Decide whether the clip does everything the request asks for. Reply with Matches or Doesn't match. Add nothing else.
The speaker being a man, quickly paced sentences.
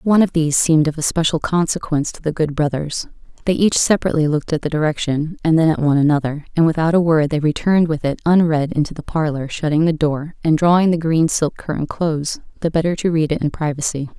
Doesn't match